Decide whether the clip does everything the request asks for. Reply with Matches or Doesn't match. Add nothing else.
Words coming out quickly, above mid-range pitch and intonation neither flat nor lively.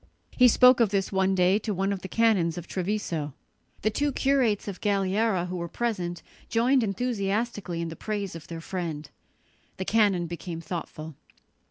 Doesn't match